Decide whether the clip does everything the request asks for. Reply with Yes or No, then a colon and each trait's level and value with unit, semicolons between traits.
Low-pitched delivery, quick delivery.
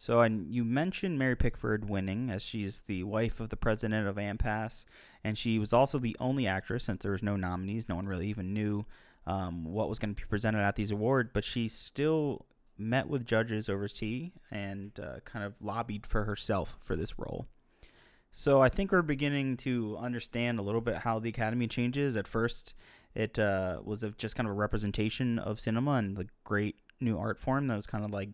Yes: low, 110 Hz; fast, 210 wpm